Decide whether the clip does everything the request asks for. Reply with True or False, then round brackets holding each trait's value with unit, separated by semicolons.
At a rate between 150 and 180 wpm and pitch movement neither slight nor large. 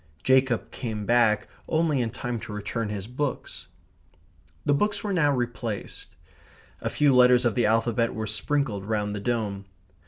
True (155 wpm; 3.6 semitones)